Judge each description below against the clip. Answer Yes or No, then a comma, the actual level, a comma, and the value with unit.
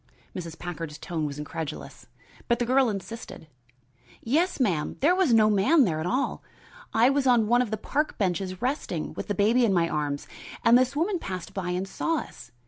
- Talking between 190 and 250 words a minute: Yes, average, 195 wpm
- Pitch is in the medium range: No, high, 215 Hz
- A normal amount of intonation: No, wide, 6.7 semitones